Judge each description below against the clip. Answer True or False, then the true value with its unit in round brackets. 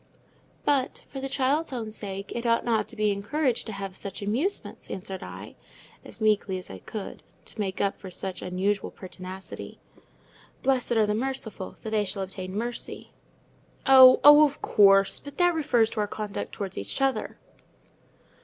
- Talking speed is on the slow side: False (165 wpm)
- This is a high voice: True (215 Hz)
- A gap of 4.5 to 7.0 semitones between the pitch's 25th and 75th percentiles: True (4.9 semitones)